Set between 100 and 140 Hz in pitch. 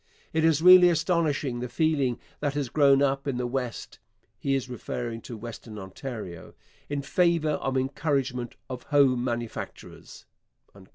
Yes: low, 135 Hz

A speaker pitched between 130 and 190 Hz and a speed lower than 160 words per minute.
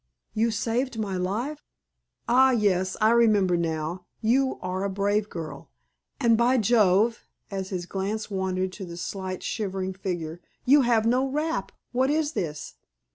No: high, 205 Hz; average, 150 wpm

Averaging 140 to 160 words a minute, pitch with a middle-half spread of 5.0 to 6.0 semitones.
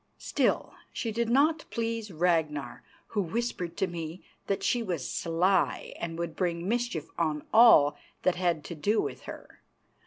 Yes: average, 155 wpm; wide, 5.6 semitones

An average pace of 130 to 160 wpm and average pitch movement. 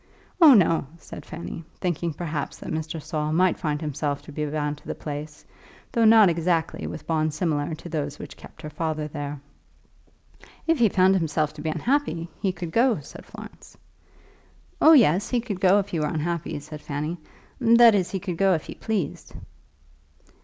No: average, 180 wpm; average, 4.1 semitones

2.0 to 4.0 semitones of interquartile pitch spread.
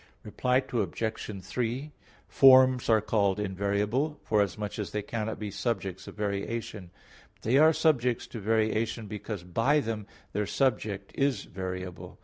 Yes: average, 3.6 semitones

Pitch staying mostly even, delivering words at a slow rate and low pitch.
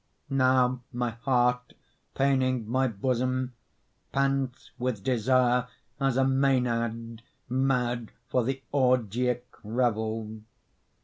Yes: narrow, 1.9 semitones; slow, 90 wpm; low, 125 Hz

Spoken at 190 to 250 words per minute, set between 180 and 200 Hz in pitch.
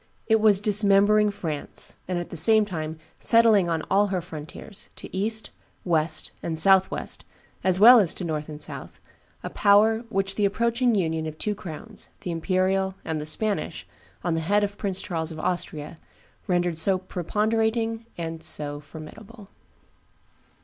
No: average, 165 wpm; high, 190 Hz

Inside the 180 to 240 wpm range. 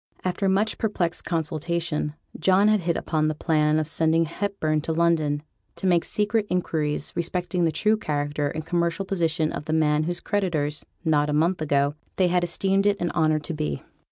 Yes: average, 185 wpm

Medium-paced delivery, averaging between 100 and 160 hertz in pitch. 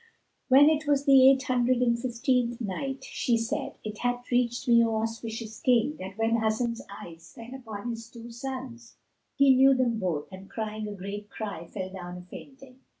No: average, 185 wpm; high, 235 Hz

